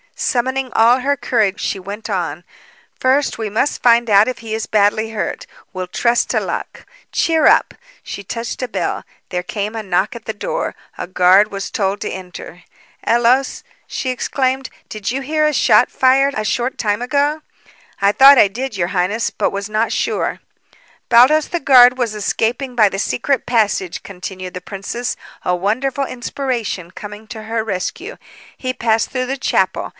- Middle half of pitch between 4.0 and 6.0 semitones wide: Yes, average, 4.4 semitones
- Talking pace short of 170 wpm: No, average, 175 wpm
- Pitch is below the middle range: No, high, 230 Hz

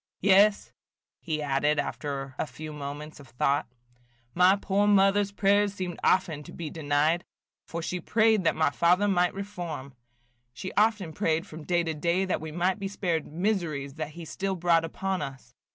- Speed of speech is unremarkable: Yes, average, 170 wpm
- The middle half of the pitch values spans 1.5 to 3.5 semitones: No, average, 4.2 semitones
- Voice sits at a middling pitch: Yes, medium, 170 Hz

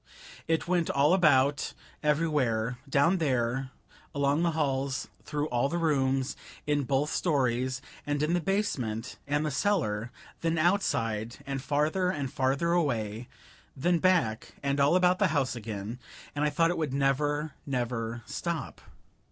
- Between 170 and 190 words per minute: No, average, 145 wpm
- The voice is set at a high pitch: No, medium, 140 Hz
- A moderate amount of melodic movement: Yes, average, 4.3 semitones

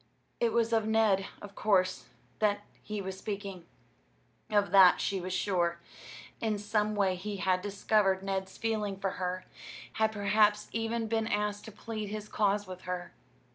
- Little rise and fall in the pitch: Yes, narrow, 2.2 semitones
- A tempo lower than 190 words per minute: Yes, average, 160 wpm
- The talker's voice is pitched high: Yes, high, 205 Hz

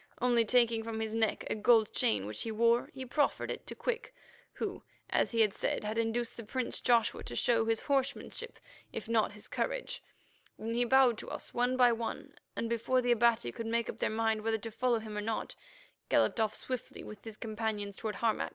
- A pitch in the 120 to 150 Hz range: No, high, 230 Hz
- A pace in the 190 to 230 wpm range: Yes, fast, 205 wpm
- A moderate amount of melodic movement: No, narrow, 1.8 semitones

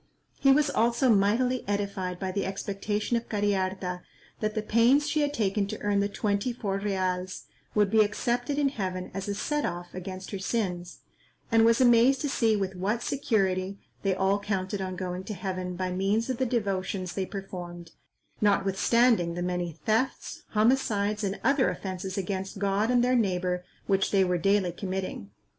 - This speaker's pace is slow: No, average, 175 wpm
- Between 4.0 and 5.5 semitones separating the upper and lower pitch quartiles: No, average, 3.5 semitones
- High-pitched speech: Yes, high, 200 Hz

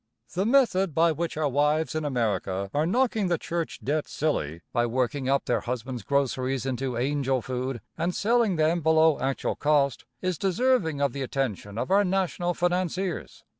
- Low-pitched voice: No, medium, 150 Hz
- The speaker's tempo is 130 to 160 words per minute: No, average, 170 wpm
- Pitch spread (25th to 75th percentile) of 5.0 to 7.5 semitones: Yes, average, 5.3 semitones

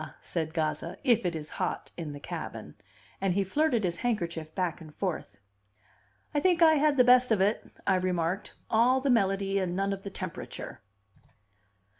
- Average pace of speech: Yes, average, 175 wpm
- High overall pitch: Yes, high, 195 Hz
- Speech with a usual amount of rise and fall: No, wide, 6.0 semitones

